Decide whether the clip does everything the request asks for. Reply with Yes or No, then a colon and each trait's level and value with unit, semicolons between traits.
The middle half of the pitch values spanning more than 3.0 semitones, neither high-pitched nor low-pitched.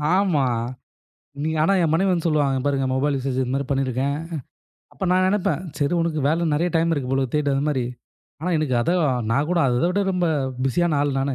Yes: average, 3.9 semitones; medium, 150 Hz